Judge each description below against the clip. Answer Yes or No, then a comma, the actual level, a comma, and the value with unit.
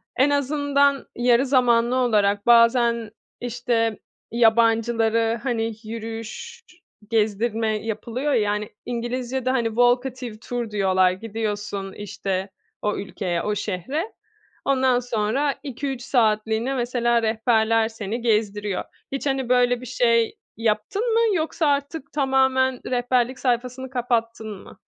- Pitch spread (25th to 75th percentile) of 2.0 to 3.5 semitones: Yes, average, 2.7 semitones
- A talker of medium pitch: No, high, 235 Hz